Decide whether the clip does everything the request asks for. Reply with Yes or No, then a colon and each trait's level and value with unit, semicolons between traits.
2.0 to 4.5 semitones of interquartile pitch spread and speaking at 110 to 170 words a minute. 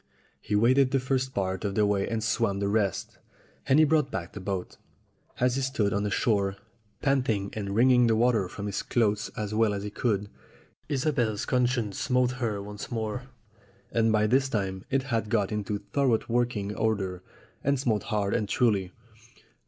No: average, 3.7 semitones; average, 185 wpm